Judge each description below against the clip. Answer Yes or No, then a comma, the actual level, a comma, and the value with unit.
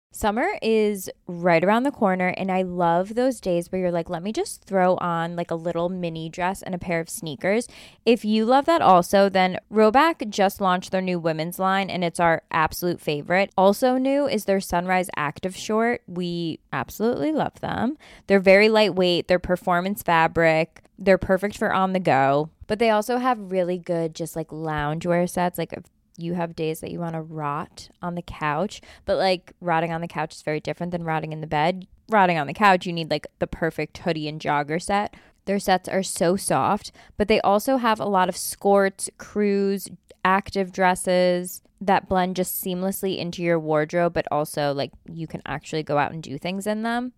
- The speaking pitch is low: No, medium, 180 Hz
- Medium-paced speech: Yes, average, 195 wpm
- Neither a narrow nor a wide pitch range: Yes, average, 3.0 semitones